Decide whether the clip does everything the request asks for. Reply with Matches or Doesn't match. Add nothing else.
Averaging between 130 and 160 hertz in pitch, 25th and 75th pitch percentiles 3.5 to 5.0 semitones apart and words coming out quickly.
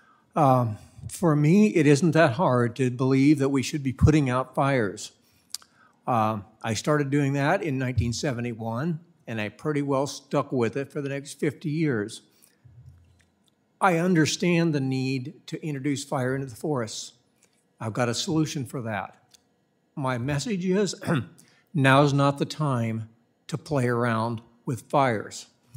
Doesn't match